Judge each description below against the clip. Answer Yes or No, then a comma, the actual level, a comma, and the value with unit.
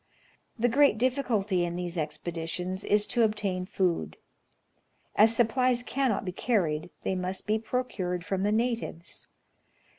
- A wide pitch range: No, average, 4.7 semitones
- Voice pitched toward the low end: No, high, 205 Hz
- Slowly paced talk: Yes, slow, 130 wpm